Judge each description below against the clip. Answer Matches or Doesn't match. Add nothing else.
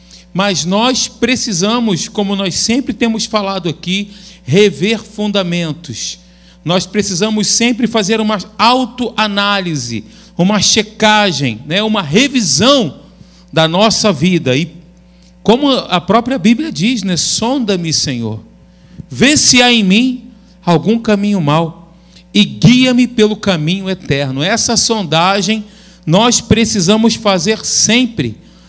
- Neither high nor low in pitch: Doesn't match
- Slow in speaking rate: Matches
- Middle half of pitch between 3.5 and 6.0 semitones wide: Matches